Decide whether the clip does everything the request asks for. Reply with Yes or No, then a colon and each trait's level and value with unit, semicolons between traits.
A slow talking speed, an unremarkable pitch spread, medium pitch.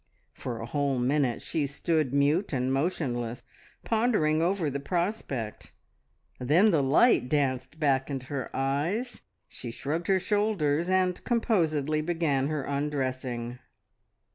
Yes: slow, 125 wpm; average, 4.6 semitones; medium, 145 Hz